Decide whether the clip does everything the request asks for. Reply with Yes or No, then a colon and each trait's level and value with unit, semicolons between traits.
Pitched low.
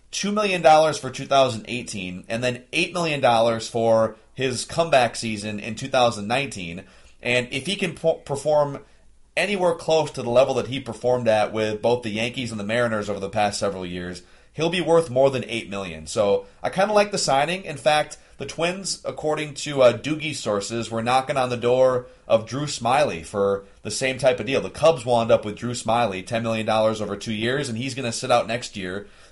Yes: low, 120 Hz